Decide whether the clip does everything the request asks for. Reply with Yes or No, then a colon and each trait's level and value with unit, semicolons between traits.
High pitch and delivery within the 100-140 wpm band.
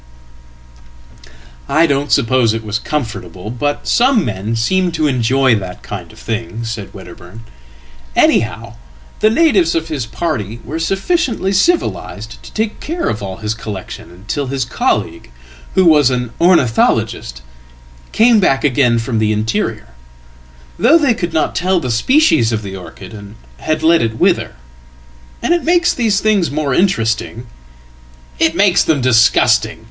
No: low, 125 Hz; slow, 135 wpm